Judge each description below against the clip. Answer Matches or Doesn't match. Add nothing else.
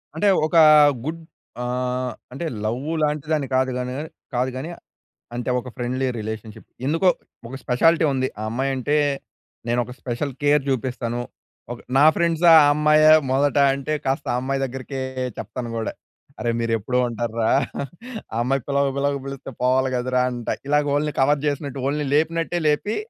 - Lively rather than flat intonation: Doesn't match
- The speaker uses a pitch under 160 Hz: Matches